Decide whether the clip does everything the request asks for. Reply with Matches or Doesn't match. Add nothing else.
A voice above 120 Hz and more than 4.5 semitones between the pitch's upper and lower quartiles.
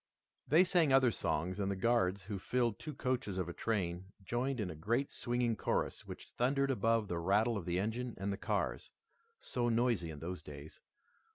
Doesn't match